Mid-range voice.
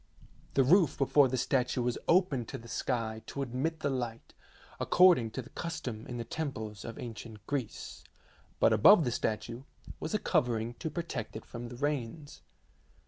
No: low, 125 Hz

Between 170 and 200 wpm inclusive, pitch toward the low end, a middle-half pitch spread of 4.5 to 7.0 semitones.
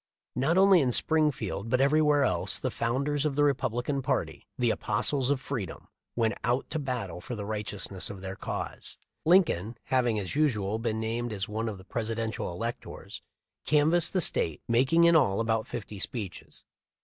Yes: average, 175 wpm; low, 120 Hz; average, 5.2 semitones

